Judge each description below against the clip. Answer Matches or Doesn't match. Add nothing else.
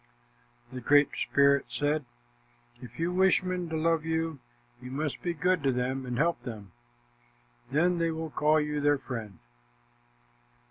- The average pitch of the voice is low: Doesn't match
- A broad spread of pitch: Doesn't match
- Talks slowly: Doesn't match